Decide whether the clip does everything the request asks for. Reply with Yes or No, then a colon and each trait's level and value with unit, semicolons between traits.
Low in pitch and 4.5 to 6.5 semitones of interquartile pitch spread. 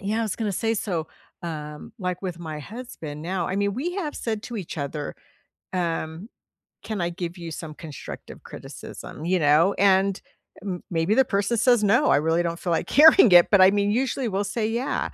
No: high, 190 Hz; average, 4.8 semitones